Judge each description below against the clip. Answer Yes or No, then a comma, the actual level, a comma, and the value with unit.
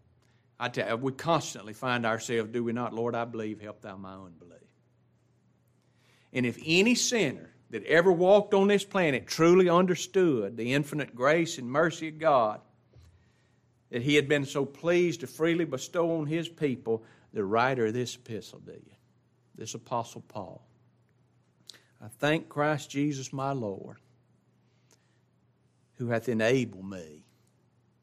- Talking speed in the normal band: Yes, average, 145 wpm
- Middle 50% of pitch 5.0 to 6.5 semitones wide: Yes, wide, 5.6 semitones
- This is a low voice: Yes, low, 125 Hz